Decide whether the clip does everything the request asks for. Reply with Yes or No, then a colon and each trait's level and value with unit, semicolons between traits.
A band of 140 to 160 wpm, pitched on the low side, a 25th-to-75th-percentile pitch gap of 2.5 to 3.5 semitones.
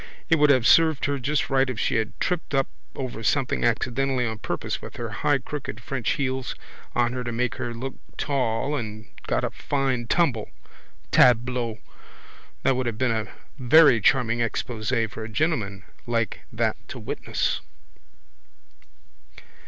Yes: average, 155 wpm; low, 125 Hz; average, 3.0 semitones